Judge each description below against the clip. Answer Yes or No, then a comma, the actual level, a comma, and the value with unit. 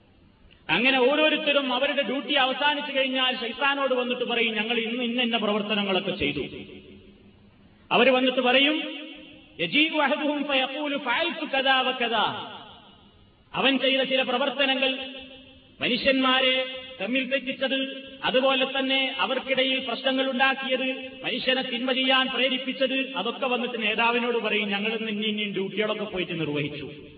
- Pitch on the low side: No, very high, 260 Hz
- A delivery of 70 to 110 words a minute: Yes, average, 95 wpm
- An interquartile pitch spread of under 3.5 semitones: Yes, average, 3.0 semitones